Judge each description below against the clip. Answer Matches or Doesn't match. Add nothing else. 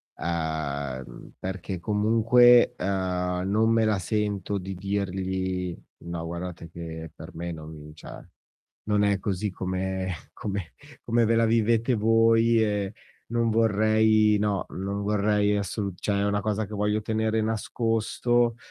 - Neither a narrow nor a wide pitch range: Matches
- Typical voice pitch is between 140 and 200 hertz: Doesn't match